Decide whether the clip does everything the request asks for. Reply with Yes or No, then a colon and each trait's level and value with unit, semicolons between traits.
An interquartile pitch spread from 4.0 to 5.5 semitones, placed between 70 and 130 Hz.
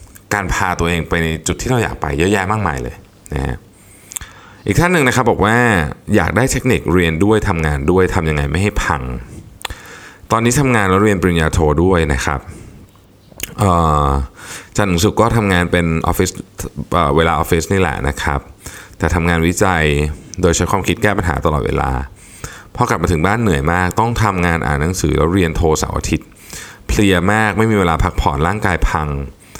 Yes: average, 4.5 semitones; very low, 90 Hz